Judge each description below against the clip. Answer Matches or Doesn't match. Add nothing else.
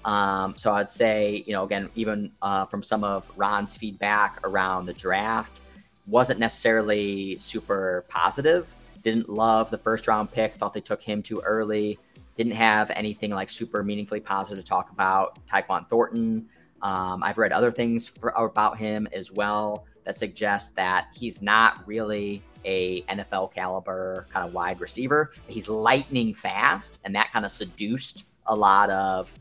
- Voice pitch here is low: Matches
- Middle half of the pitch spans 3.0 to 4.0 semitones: Doesn't match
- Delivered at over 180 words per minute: Doesn't match